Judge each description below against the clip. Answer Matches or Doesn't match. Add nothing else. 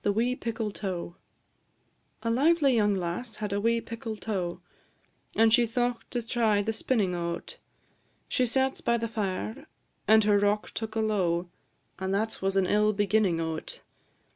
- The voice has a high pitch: Matches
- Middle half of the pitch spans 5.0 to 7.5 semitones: Doesn't match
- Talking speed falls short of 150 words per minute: Matches